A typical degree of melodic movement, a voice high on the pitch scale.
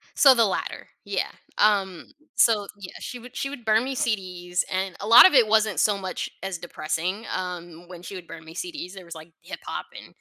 Yes: average, 4.1 semitones; high, 195 Hz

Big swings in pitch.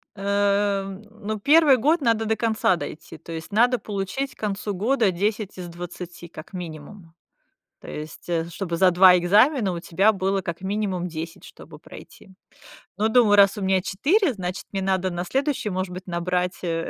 No: average, 3.4 semitones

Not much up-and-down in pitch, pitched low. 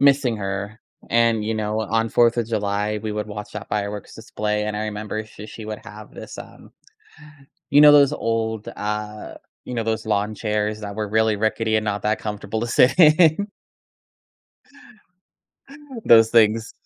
Yes: narrow, 1.3 semitones; low, 110 Hz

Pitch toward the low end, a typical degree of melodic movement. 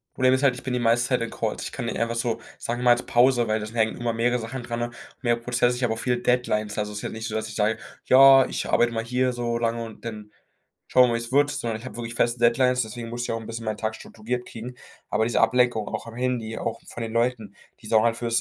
No: low, 120 Hz; narrow, 1.6 semitones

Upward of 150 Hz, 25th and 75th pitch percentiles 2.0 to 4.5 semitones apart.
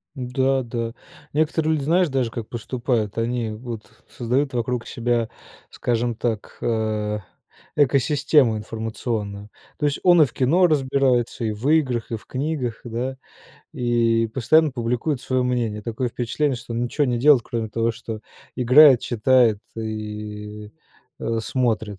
No: low, 120 Hz; average, 2.9 semitones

